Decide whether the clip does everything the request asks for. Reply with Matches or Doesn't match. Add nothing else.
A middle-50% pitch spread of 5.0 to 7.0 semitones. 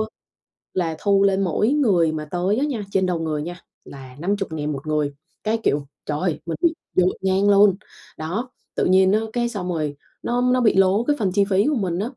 Doesn't match